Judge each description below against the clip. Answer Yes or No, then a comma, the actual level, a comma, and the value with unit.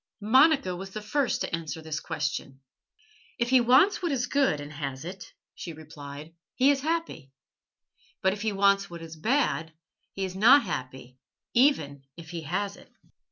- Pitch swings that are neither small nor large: No, wide, 8.4 semitones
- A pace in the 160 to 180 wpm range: Yes, average, 170 wpm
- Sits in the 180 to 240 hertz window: Yes, high, 190 Hz